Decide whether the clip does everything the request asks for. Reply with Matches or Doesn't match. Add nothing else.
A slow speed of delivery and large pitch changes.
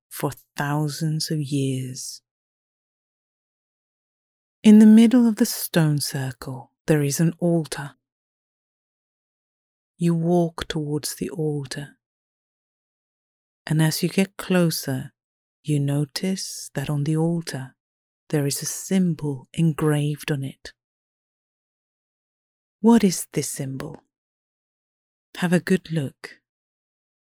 Doesn't match